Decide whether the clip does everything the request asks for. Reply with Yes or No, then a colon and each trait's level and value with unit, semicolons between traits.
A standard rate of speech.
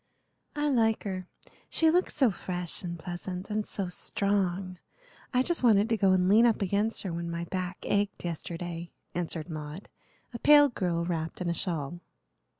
Yes: average, 170 wpm